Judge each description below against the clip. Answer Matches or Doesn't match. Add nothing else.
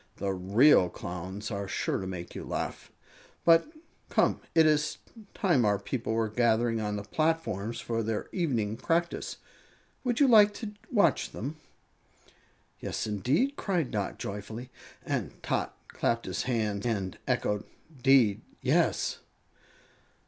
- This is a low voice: Matches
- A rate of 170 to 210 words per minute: Doesn't match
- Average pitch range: Doesn't match